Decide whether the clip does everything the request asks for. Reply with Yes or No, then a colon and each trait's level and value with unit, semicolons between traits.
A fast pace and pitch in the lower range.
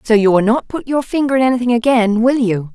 No: fast, 260 wpm; high, 235 Hz